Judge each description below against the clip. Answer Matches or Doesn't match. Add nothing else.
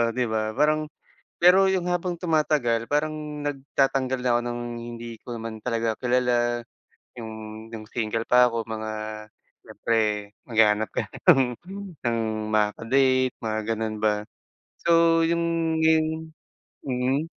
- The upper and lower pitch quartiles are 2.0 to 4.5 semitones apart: Doesn't match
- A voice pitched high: Doesn't match